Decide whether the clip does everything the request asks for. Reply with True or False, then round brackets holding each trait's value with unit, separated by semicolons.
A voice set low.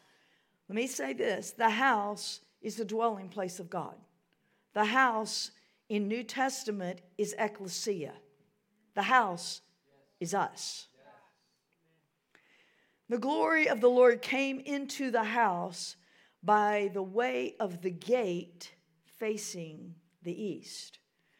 False (210 Hz)